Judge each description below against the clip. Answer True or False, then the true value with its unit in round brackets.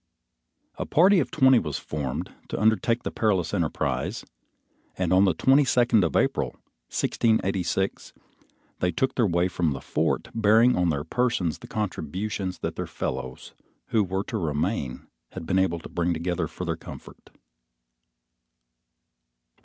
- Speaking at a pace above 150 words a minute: False (145 wpm)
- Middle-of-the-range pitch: False (95 Hz)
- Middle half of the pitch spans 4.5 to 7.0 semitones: True (5.0 semitones)